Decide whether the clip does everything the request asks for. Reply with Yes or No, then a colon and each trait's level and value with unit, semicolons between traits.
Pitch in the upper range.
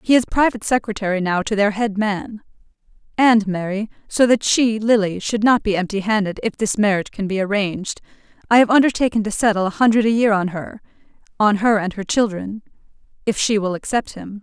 Yes: high, 210 Hz